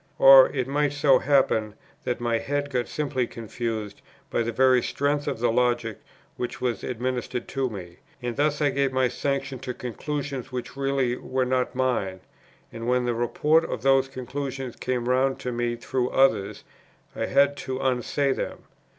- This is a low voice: Yes, low, 130 Hz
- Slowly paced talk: No, average, 170 wpm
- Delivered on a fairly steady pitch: Yes, narrow, 2.1 semitones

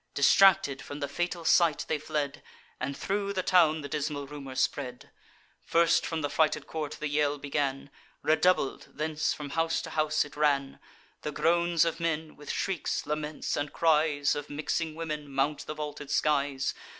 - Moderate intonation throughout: No, narrow, 2.2 semitones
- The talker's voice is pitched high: No, medium, 150 Hz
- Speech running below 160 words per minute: No, average, 165 wpm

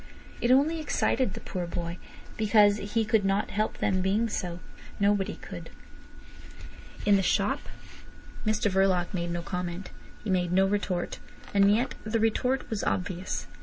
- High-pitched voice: Yes, high, 200 Hz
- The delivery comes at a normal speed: Yes, average, 160 wpm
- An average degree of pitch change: Yes, average, 3.1 semitones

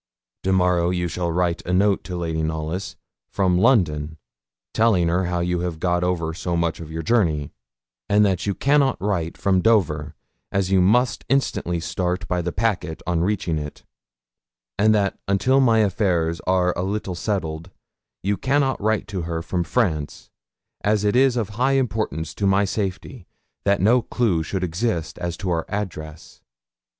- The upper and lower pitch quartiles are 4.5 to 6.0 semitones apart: No, average, 3.6 semitones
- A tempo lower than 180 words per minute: Yes, average, 165 wpm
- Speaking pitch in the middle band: No, very low, 90 Hz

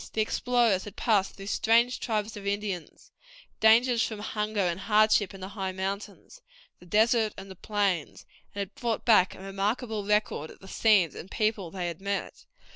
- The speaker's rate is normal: Yes, average, 180 wpm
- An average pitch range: No, narrow, 2.3 semitones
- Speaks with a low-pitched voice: No, high, 205 Hz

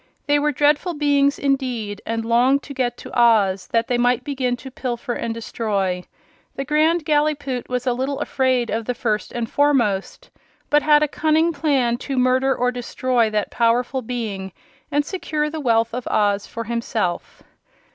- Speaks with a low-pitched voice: No, very high, 250 Hz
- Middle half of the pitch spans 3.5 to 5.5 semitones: Yes, average, 3.8 semitones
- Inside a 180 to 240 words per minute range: No, average, 170 wpm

